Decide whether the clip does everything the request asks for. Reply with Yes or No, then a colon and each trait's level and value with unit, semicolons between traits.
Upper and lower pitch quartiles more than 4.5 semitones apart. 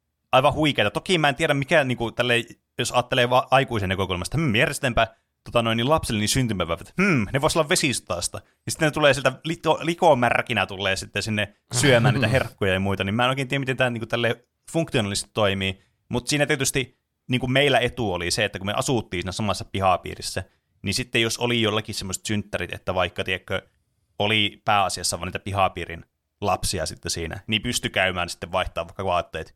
Yes: average, 5.2 semitones